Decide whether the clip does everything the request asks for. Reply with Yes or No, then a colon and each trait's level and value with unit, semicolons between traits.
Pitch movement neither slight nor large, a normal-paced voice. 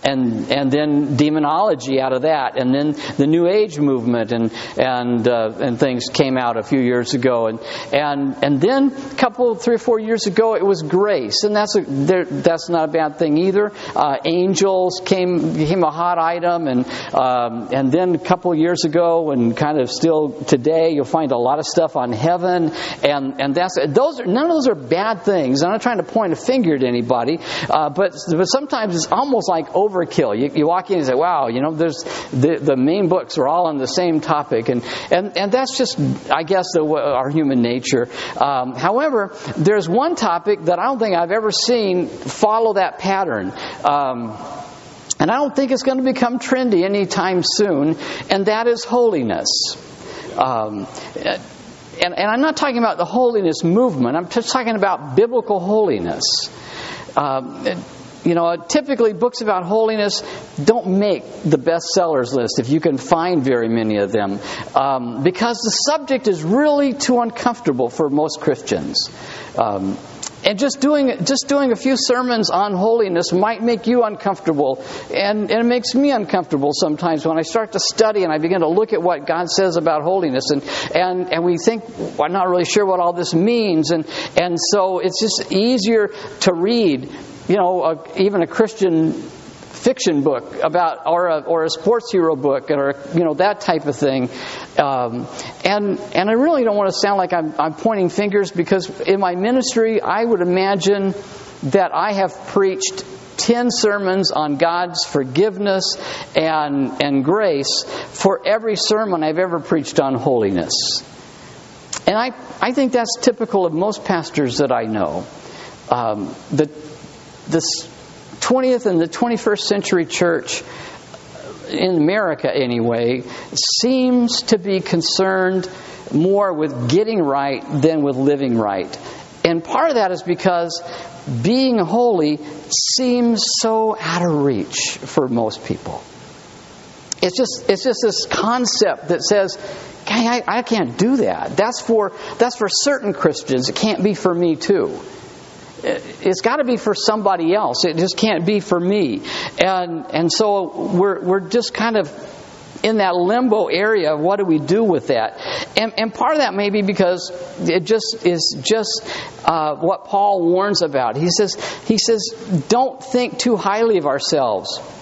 No: wide, 5.8 semitones; average, 175 wpm